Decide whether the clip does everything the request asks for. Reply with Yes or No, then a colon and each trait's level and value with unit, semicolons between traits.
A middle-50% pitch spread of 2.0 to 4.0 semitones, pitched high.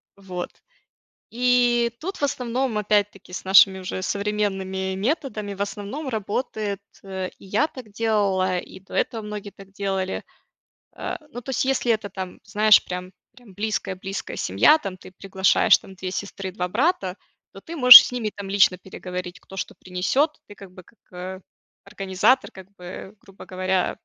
Yes: average, 3.2 semitones; high, 200 Hz